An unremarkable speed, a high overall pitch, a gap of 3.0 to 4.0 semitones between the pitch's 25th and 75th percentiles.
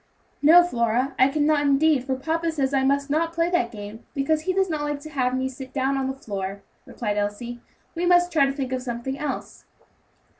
No: fast, 215 wpm; very high, 275 Hz; average, 3.7 semitones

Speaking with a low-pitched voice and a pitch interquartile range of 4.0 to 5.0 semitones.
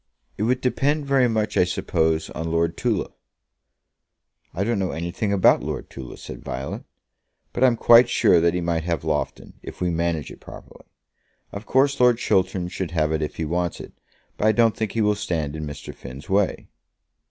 No: very low, 90 Hz; wide, 5.5 semitones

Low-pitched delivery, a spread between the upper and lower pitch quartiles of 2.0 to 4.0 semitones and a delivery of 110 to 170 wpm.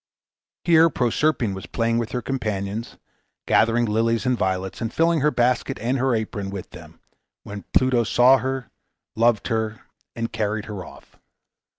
Yes: low, 115 Hz; average, 3.4 semitones; average, 155 wpm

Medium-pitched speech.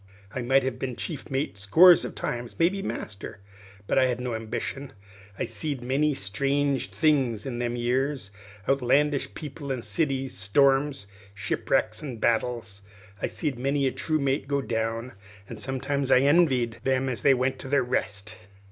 No: low, 130 Hz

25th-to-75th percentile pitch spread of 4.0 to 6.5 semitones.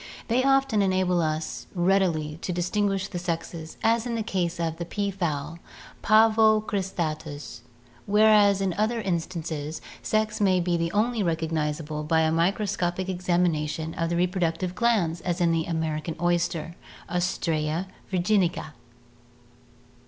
No: average, 3.6 semitones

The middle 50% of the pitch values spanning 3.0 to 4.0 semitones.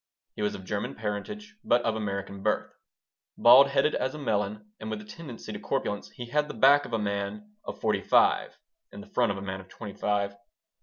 No: wide, 5.4 semitones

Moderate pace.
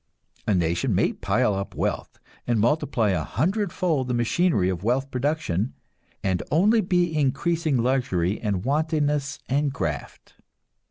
No: slow, 130 wpm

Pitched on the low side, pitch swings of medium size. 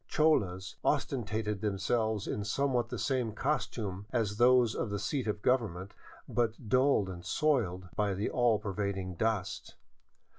Yes: low, 110 Hz; average, 3.6 semitones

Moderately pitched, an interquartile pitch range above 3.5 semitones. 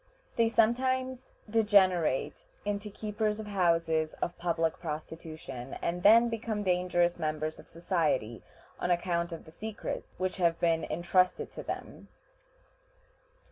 Yes: medium, 175 Hz; average, 4.3 semitones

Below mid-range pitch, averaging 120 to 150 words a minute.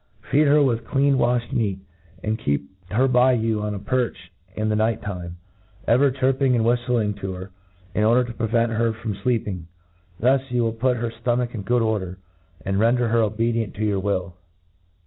No: low, 115 Hz; average, 190 wpm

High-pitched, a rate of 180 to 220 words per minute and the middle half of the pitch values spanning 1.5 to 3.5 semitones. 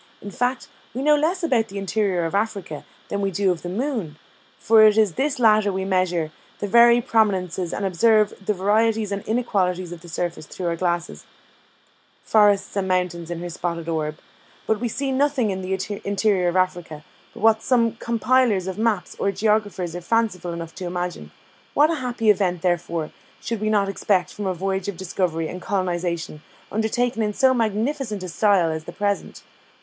No: high, 200 Hz; average, 185 wpm; average, 4.0 semitones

